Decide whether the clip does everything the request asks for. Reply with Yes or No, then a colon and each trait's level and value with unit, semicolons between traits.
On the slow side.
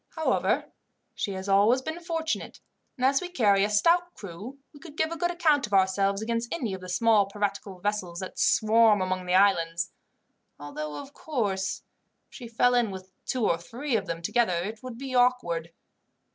No: average, 185 wpm